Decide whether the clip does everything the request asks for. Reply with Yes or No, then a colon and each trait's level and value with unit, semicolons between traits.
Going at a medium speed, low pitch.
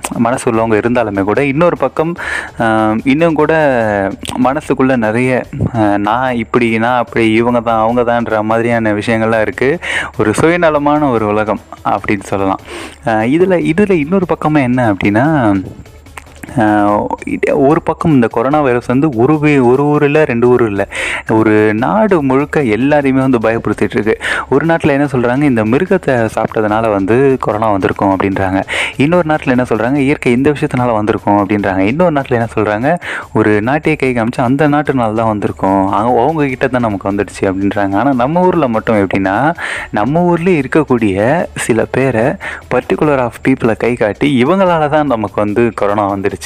No: fast, 140 wpm; low, 120 Hz